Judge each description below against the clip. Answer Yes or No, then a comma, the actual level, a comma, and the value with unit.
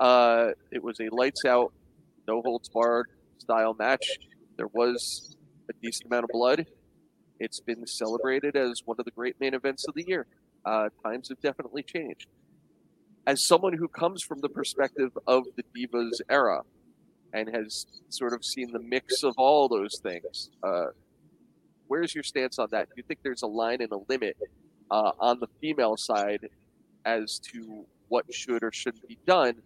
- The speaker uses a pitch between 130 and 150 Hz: No, low, 120 Hz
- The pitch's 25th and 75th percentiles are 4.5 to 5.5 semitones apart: No, average, 2.9 semitones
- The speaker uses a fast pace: No, average, 175 wpm